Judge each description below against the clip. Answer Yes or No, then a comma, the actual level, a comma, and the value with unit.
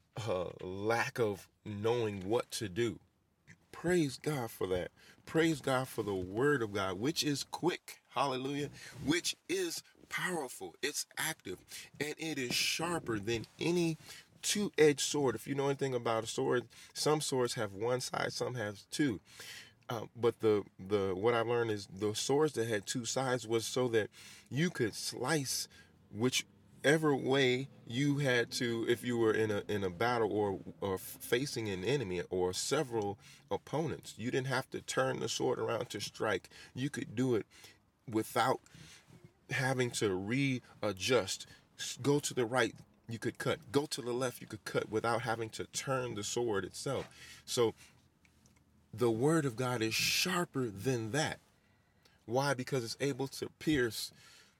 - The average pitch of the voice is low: Yes, low, 125 Hz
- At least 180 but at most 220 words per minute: No, average, 160 wpm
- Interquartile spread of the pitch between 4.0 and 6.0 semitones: Yes, average, 4.3 semitones